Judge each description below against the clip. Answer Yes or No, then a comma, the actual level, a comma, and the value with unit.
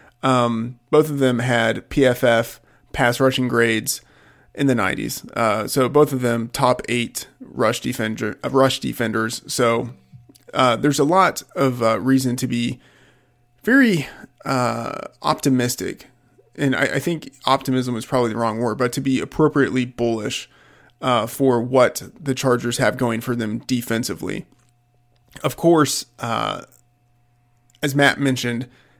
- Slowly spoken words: No, average, 145 wpm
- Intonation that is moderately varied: No, narrow, 2.2 semitones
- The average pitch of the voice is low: Yes, low, 125 Hz